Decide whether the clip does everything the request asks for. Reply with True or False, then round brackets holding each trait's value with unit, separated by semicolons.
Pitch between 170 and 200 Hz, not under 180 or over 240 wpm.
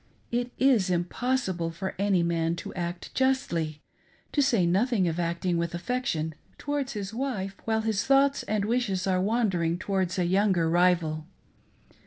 False (190 Hz; 150 wpm)